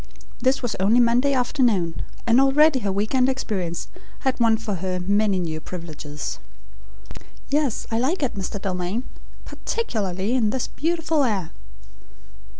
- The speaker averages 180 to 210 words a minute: No, average, 140 wpm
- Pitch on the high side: Yes, high, 225 Hz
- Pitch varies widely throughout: Yes, wide, 5.8 semitones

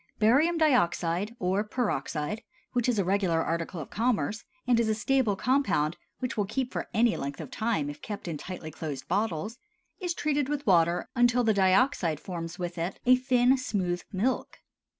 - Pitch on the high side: Yes, high, 210 Hz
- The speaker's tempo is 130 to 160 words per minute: No, average, 175 wpm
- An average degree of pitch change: No, wide, 6.3 semitones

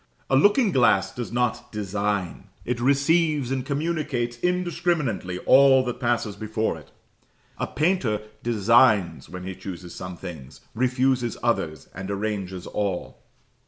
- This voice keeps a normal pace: No, slow, 125 wpm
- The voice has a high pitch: No, low, 120 Hz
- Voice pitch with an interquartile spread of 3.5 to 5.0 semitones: No, wide, 5.5 semitones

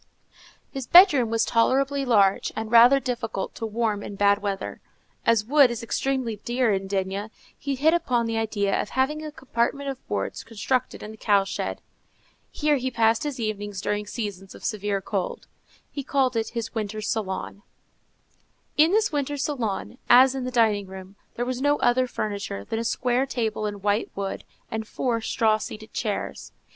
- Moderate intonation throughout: Yes, average, 4.0 semitones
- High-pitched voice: Yes, high, 230 Hz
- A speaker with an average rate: Yes, average, 175 wpm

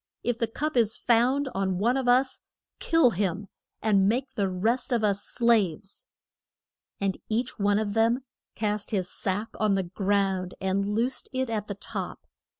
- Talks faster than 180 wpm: No, average, 165 wpm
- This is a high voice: Yes, high, 215 Hz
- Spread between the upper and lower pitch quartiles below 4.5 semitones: Yes, average, 3.5 semitones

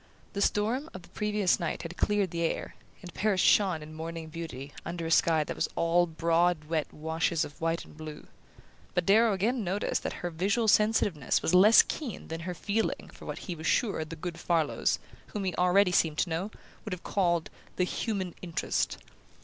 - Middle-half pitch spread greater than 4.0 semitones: No, average, 3.6 semitones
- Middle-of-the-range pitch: Yes, medium, 175 Hz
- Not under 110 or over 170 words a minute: No, average, 195 wpm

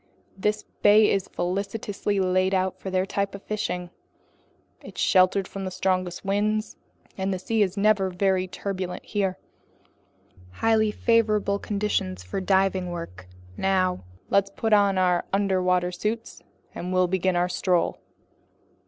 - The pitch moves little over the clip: Yes, narrow, 1.9 semitones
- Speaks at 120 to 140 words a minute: Yes, slow, 135 wpm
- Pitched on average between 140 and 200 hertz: Yes, high, 190 Hz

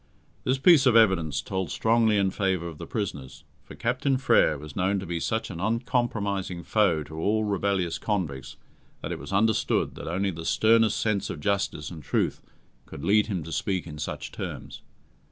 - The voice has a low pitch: Yes, low, 100 Hz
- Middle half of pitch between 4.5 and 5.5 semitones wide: Yes, average, 4.9 semitones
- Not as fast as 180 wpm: No, average, 185 wpm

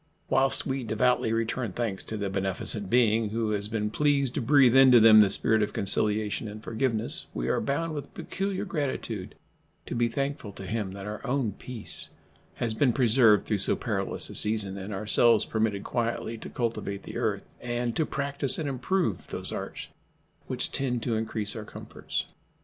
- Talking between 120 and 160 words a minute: No, average, 180 wpm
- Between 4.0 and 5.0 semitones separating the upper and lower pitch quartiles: No, average, 3.5 semitones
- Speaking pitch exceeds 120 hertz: No, low, 115 Hz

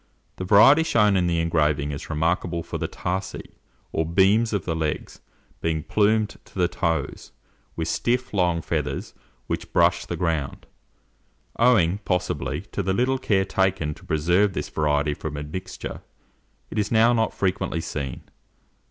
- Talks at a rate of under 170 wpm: Yes, average, 150 wpm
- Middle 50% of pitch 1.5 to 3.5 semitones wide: No, average, 4.6 semitones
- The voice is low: Yes, very low, 90 Hz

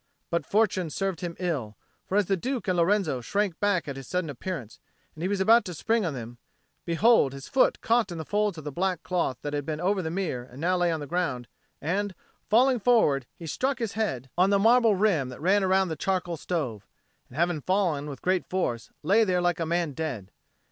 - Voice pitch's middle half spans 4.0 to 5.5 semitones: Yes, average, 5.2 semitones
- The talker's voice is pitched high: No, medium, 175 Hz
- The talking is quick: Yes, fast, 225 wpm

